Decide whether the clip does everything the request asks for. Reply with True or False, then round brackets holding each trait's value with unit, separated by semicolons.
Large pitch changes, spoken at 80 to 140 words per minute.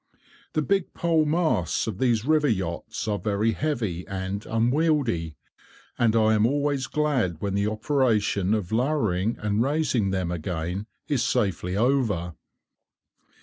True (6.4 semitones; 135 wpm)